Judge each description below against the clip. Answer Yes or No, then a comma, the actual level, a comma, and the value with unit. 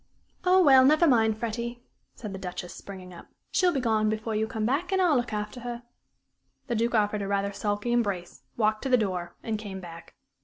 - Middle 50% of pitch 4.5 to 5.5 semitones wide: No, average, 3.3 semitones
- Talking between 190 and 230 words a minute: Yes, fast, 205 wpm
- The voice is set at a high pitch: Yes, high, 220 Hz